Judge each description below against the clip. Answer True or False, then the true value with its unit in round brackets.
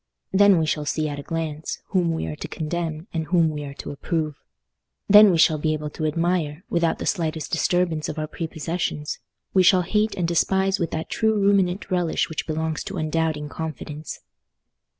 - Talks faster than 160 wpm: True (190 wpm)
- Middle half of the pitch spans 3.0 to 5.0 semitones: False (2.6 semitones)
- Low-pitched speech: False (165 Hz)